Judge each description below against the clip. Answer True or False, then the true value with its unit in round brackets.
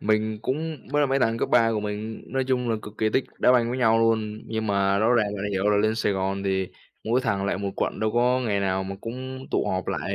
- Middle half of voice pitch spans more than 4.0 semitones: False (3.4 semitones)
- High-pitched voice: False (110 Hz)